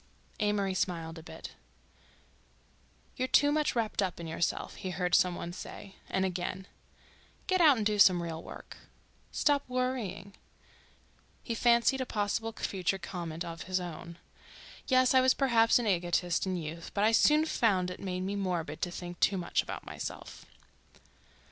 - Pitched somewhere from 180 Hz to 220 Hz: Yes, high, 190 Hz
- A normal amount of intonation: Yes, average, 4.8 semitones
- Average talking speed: Yes, average, 160 wpm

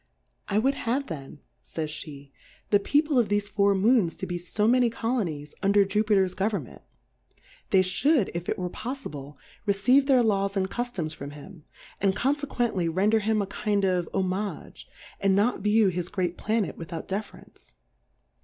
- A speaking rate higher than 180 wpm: No, average, 165 wpm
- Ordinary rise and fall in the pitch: Yes, average, 3.9 semitones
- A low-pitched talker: No, high, 200 Hz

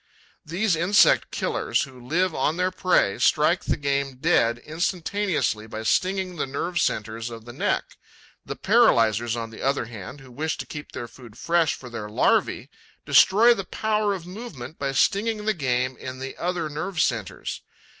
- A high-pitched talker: No, medium, 145 Hz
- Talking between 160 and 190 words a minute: Yes, average, 170 wpm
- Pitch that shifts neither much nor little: No, wide, 7.3 semitones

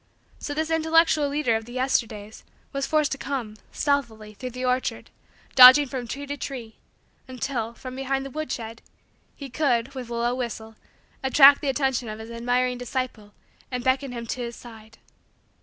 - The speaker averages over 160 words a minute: Yes, average, 170 wpm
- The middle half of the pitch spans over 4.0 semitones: No, average, 2.9 semitones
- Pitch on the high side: Yes, very high, 255 Hz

